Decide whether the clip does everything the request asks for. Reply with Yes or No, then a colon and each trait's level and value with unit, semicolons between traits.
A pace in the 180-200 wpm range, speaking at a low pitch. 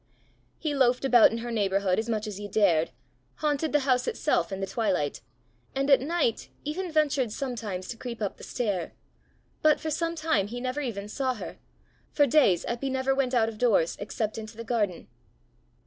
No: average, 190 wpm; high, 235 Hz